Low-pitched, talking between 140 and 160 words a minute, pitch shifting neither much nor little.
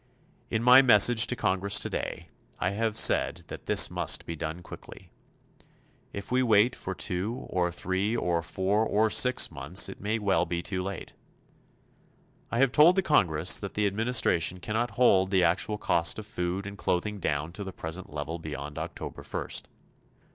No: very low, 95 Hz; average, 170 wpm; average, 4.1 semitones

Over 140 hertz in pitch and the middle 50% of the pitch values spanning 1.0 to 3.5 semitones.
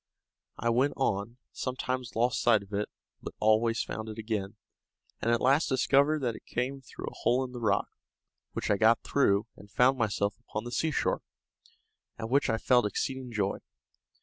No: low, 115 Hz; average, 3.1 semitones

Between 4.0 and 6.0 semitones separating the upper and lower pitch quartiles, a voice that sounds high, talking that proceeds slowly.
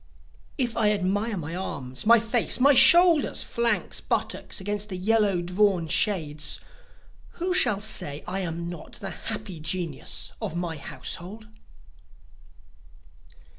Yes: average, 4.5 semitones; high, 195 Hz; slow, 125 wpm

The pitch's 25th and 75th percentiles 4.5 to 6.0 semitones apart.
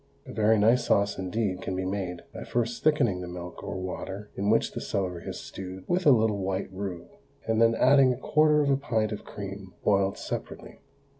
No: average, 3.7 semitones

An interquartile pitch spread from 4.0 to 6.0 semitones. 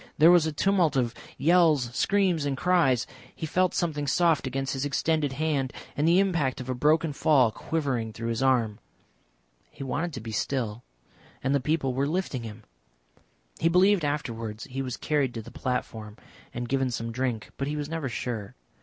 Yes: average, 4.5 semitones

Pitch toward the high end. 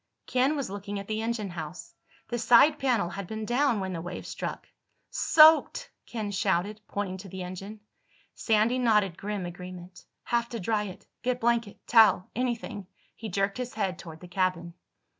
Yes: high, 205 Hz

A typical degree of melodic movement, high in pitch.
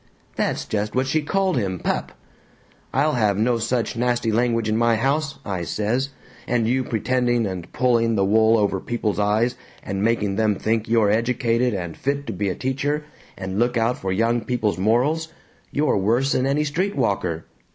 No: average, 3.5 semitones; low, 115 Hz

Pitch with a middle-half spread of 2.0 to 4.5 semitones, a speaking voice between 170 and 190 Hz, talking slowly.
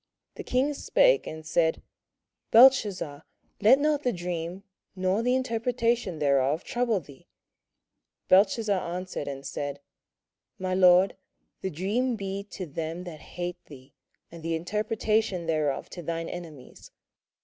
No: wide, 5.6 semitones; medium, 185 Hz; slow, 125 wpm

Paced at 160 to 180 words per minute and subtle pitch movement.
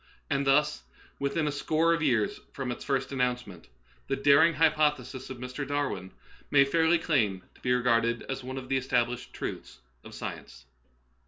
No: average, 165 wpm; average, 3.0 semitones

